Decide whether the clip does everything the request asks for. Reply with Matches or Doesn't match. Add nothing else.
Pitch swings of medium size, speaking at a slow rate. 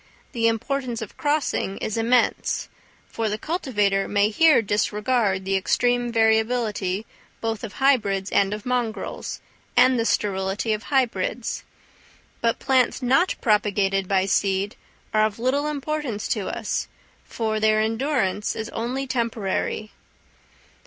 Matches